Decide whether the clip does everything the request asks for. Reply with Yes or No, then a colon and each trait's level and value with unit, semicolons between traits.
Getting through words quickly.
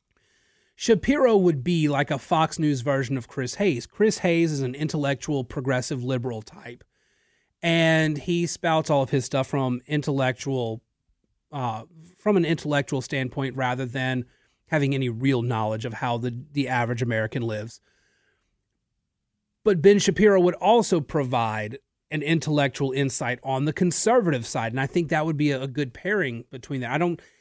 No: average, 160 wpm